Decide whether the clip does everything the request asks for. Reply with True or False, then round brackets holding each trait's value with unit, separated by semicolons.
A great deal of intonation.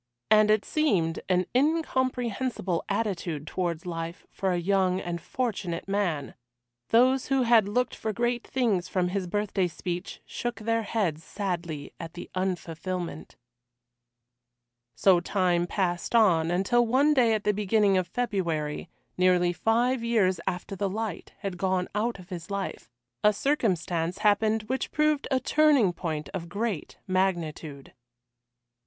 False (4.6 semitones)